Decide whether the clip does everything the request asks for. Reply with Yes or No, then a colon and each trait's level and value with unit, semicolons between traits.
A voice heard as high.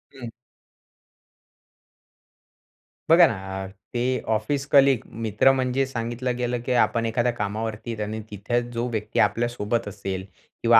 No: low, 120 Hz